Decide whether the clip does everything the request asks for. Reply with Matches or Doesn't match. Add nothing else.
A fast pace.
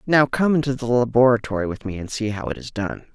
Matches